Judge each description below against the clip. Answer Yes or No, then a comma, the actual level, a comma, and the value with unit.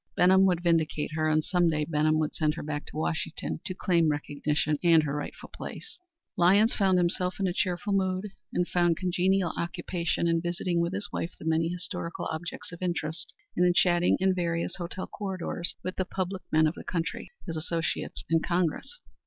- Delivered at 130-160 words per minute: No, average, 190 wpm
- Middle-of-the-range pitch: Yes, medium, 175 Hz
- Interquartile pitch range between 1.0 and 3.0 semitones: Yes, narrow, 2.4 semitones